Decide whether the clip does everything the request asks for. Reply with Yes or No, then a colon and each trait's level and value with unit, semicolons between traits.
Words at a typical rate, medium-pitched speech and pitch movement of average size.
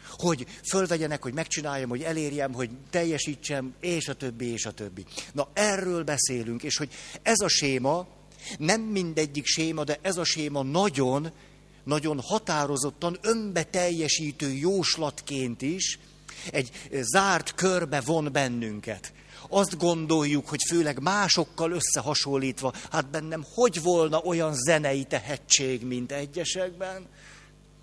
Yes: average, 120 wpm; medium, 155 Hz; average, 3.8 semitones